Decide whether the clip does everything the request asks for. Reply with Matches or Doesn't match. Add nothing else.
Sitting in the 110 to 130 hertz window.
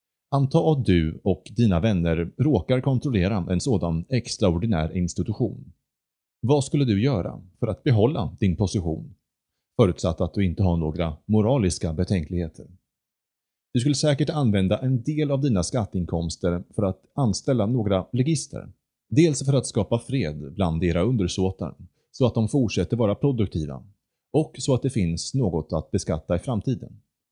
Doesn't match